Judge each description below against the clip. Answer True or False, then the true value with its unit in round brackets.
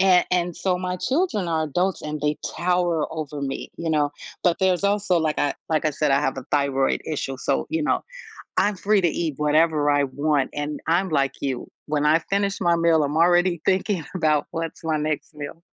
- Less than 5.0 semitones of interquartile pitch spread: True (3.5 semitones)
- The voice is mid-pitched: True (160 Hz)